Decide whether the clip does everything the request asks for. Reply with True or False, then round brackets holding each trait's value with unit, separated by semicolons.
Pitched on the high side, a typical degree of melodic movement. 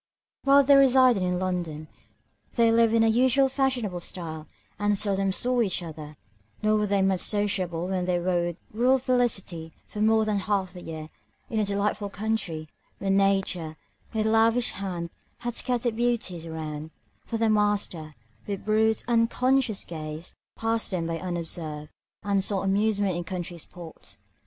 True (200 Hz; 4.4 semitones)